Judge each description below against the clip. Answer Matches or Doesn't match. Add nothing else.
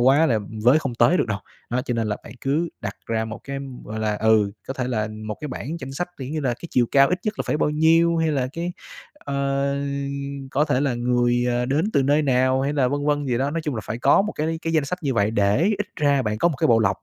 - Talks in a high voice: Doesn't match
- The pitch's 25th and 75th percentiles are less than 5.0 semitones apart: Matches